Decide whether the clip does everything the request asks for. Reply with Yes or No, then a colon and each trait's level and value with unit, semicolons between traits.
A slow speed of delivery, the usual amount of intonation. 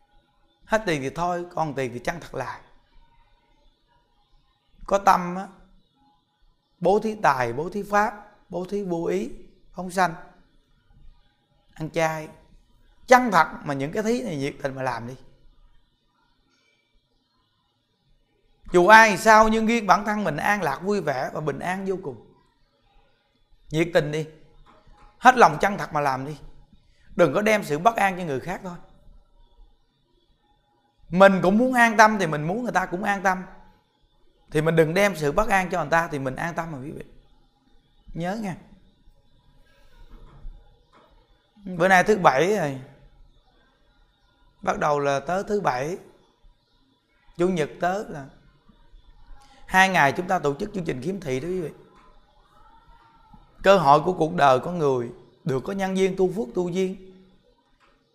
No: slow, 155 wpm; wide, 5.7 semitones